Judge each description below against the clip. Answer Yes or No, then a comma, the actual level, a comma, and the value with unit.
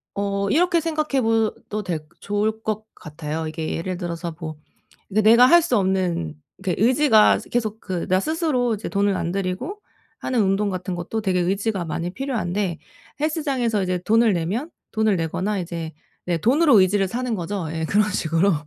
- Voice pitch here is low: No, high, 200 Hz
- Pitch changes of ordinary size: Yes, average, 4.6 semitones